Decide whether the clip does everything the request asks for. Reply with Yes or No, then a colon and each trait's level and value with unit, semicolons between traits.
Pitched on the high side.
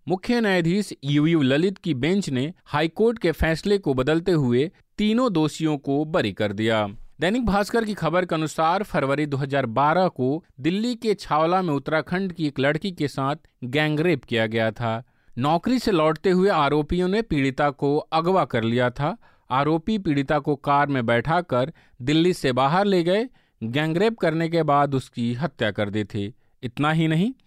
No: medium, 155 Hz